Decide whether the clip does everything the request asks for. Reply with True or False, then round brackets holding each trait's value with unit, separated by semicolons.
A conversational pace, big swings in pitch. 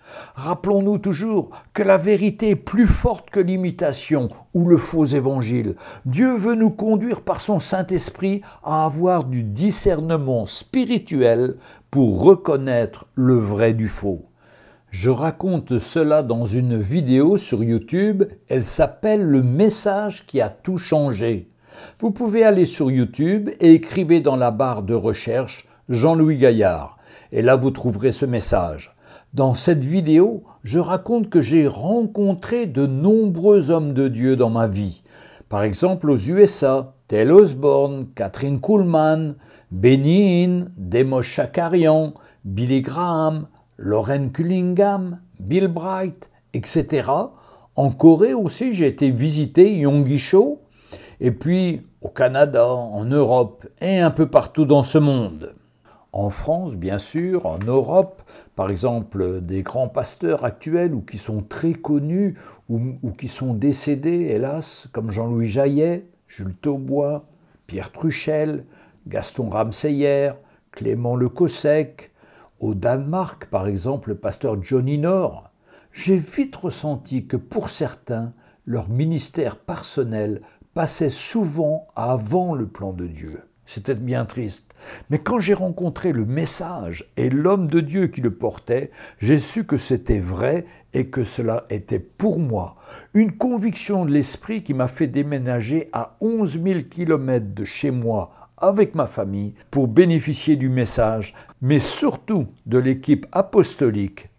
False (135 wpm; 6.5 semitones)